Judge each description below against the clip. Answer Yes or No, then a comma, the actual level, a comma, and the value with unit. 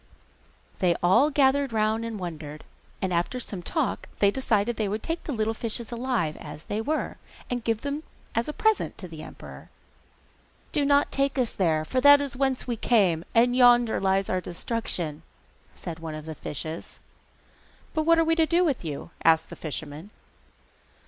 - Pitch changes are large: Yes, wide, 7.5 semitones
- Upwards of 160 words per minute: Yes, average, 180 wpm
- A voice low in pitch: No, high, 225 Hz